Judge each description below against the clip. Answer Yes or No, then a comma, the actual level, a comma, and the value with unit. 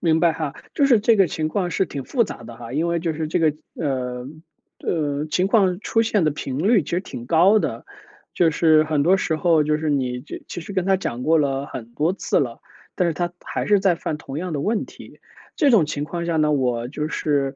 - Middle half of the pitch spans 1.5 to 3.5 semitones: No, average, 4.2 semitones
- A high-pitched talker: No, medium, 160 Hz